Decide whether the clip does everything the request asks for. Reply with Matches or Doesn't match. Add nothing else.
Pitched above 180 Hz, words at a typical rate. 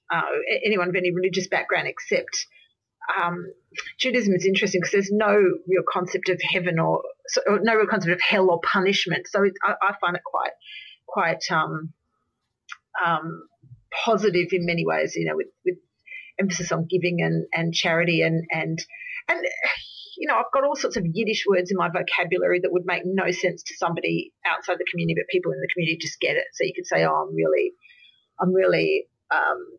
Matches